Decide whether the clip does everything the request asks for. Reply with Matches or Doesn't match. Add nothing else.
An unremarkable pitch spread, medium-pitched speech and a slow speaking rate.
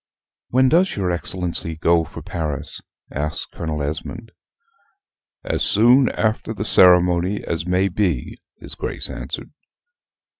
Doesn't match